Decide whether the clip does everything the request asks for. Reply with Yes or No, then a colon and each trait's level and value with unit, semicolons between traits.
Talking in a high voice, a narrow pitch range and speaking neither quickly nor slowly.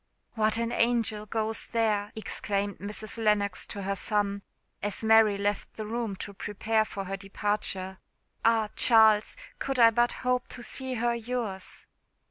Yes: high, 215 Hz; narrow, 2.1 semitones; average, 150 wpm